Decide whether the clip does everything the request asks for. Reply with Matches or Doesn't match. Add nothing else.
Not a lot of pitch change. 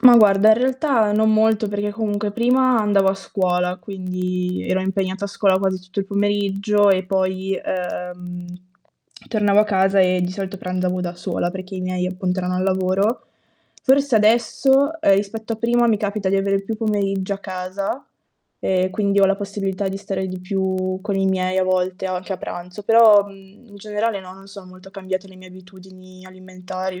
Matches